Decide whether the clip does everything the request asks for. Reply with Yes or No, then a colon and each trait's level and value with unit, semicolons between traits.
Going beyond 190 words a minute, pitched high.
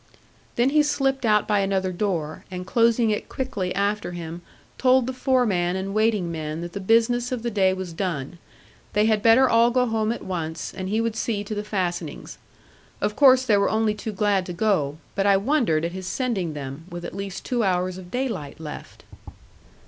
Yes: average, 200 wpm; high, 205 Hz